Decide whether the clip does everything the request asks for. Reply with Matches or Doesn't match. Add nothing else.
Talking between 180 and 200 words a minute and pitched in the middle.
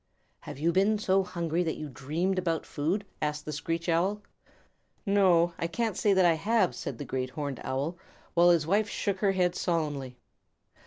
Matches